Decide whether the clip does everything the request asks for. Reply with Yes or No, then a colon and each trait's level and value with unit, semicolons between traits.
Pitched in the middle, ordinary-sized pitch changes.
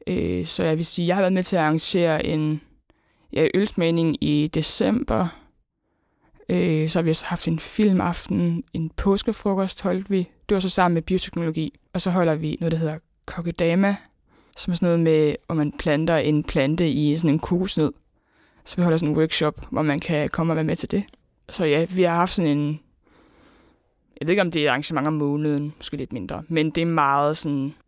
Yes: medium, 160 Hz; average, 3.0 semitones